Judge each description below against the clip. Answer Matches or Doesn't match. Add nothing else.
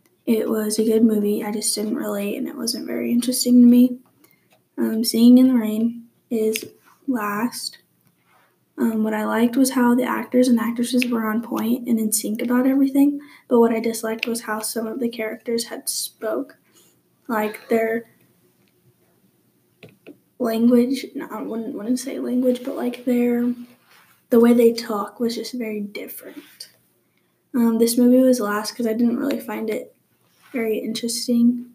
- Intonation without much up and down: Matches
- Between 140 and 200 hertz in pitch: Doesn't match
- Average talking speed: Matches